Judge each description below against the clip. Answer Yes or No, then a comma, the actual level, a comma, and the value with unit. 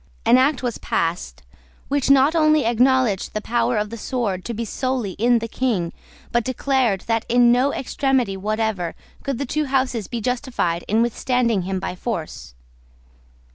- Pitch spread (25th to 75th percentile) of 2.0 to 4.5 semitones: Yes, average, 4.0 semitones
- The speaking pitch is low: No, high, 235 Hz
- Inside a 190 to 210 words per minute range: No, average, 165 wpm